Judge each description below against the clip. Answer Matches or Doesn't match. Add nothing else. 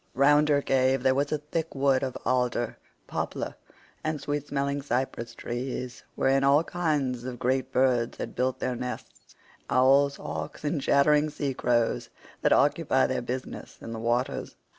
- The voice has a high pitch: Doesn't match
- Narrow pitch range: Matches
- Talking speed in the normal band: Matches